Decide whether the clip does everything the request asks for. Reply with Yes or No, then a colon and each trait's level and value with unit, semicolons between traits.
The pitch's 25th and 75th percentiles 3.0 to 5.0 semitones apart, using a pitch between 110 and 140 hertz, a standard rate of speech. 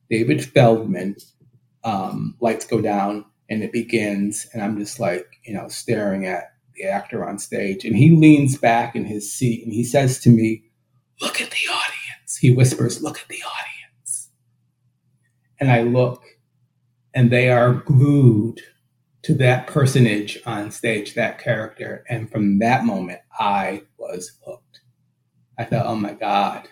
No: narrow, 2.4 semitones; low, 120 Hz; average, 155 wpm